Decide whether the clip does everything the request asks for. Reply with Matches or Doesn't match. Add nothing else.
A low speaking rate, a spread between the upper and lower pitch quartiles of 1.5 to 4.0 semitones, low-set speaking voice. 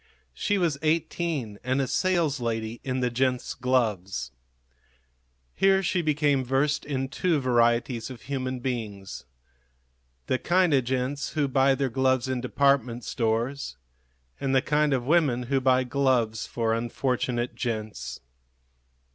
Matches